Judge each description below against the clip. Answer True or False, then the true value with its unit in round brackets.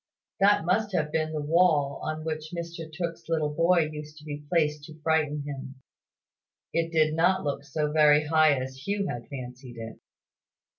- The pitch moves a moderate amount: False (2.1 semitones)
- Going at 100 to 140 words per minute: False (170 wpm)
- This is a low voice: False (155 Hz)